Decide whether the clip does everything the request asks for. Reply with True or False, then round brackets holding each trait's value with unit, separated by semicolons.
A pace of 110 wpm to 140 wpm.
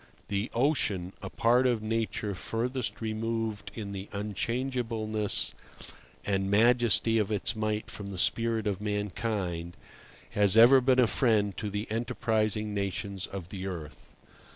True (135 wpm)